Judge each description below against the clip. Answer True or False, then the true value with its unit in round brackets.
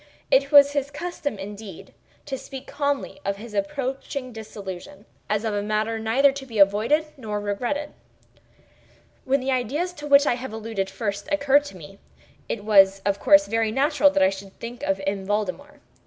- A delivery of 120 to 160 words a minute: False (175 wpm)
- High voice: True (230 Hz)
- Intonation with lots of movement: True (5.7 semitones)